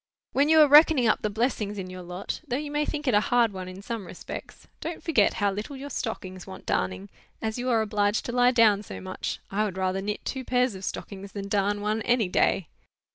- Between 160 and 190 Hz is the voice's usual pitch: No, high, 210 Hz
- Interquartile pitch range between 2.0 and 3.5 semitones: No, average, 4.3 semitones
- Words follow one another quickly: Yes, fast, 225 wpm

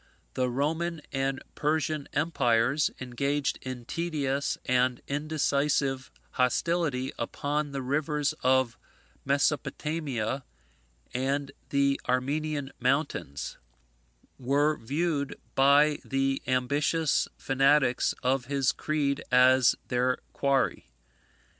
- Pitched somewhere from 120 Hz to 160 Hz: Yes, medium, 140 Hz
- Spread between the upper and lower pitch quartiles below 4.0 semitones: Yes, narrow, 2.5 semitones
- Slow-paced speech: Yes, slow, 90 wpm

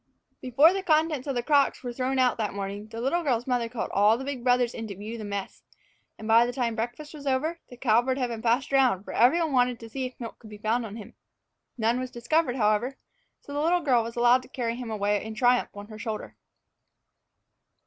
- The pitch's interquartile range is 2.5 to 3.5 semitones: Yes, average, 3.0 semitones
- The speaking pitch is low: No, high, 245 Hz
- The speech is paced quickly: Yes, fast, 240 wpm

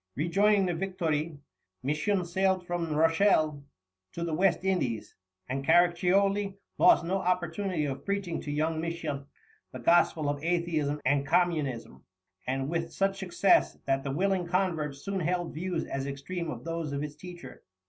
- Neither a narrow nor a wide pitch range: Yes, average, 3.7 semitones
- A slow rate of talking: No, average, 150 wpm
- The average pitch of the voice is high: No, medium, 170 Hz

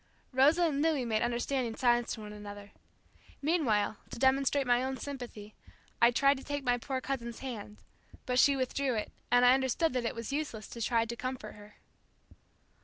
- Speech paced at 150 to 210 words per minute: Yes, average, 180 wpm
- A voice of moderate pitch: No, very high, 250 Hz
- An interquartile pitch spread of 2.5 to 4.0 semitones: Yes, average, 3.0 semitones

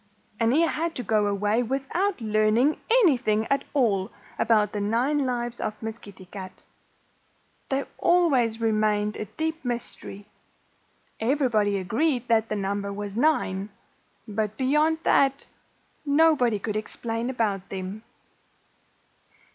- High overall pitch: Yes, high, 225 Hz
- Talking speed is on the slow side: Yes, slow, 125 wpm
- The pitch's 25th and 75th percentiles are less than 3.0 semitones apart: No, average, 4.5 semitones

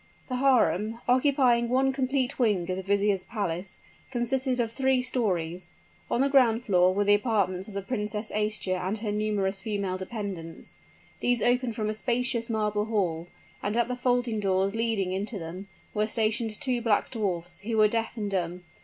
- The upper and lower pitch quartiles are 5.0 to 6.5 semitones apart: No, average, 3.8 semitones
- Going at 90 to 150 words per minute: No, average, 175 wpm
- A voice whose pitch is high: Yes, high, 215 Hz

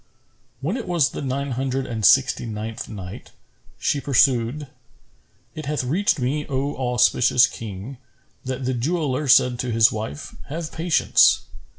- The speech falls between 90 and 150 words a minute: Yes, average, 145 wpm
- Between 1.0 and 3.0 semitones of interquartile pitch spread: No, average, 3.4 semitones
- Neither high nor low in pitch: No, low, 130 Hz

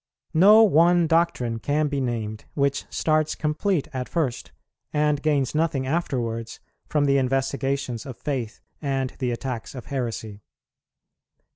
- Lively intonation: No, average, 3.6 semitones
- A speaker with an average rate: No, slow, 130 wpm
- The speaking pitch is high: No, medium, 140 Hz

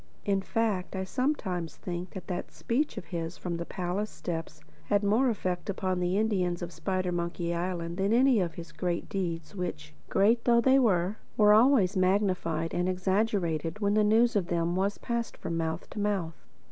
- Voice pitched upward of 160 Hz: Yes, medium, 185 Hz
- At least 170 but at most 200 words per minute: Yes, average, 185 wpm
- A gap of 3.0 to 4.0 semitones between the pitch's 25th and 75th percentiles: Yes, average, 3.4 semitones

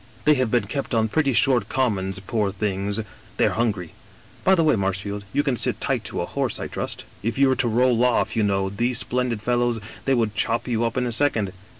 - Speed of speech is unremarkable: No, fast, 240 wpm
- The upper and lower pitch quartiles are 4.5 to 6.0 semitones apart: No, average, 3.7 semitones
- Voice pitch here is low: Yes, low, 115 Hz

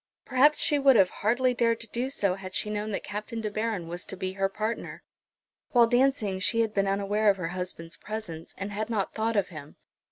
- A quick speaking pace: Yes, fast, 220 wpm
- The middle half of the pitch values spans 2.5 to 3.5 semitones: Yes, average, 3.2 semitones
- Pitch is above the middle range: Yes, high, 210 Hz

